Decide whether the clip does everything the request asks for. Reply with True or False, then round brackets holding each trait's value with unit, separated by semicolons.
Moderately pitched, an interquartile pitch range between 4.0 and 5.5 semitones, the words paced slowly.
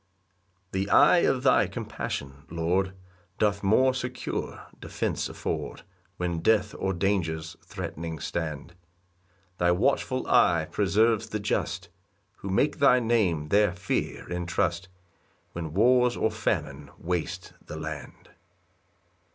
False (95 Hz; 4.8 semitones; 120 wpm)